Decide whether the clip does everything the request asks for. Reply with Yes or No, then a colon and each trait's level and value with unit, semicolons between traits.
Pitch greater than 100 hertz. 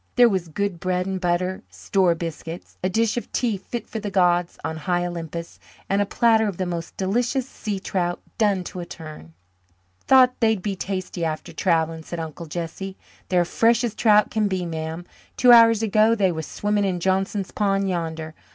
Yes: medium, 185 Hz